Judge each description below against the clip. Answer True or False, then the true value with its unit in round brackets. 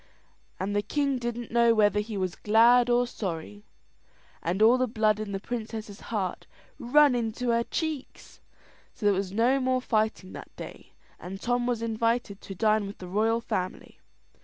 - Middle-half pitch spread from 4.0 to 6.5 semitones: False (3.0 semitones)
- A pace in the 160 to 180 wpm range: True (170 wpm)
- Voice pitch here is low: False (225 Hz)